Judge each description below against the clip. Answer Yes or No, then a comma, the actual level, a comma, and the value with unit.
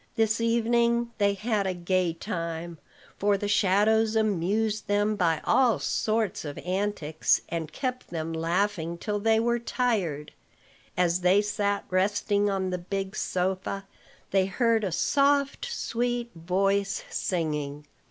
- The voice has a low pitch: No, high, 200 Hz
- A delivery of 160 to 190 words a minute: No, slow, 135 wpm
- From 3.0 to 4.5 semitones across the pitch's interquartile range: Yes, average, 3.9 semitones